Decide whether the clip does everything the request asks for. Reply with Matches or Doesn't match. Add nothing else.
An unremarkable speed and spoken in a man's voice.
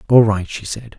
Doesn't match